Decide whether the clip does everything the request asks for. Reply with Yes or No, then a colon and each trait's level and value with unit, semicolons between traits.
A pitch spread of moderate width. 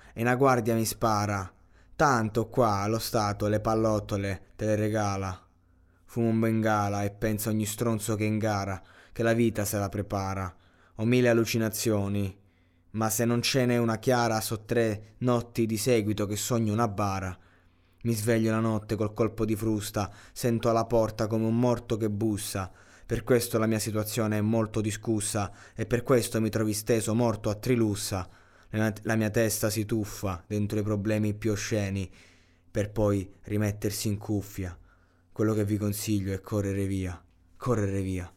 No: narrow, 2.3 semitones